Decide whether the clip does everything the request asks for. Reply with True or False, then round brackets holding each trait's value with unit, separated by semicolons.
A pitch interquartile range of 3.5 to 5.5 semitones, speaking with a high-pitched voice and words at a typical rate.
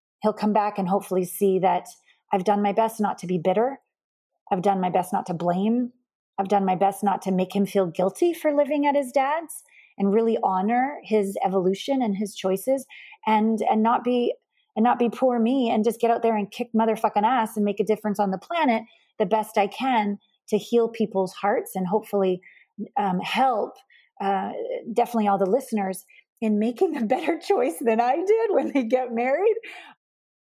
True (4.4 semitones; 220 Hz; 195 wpm)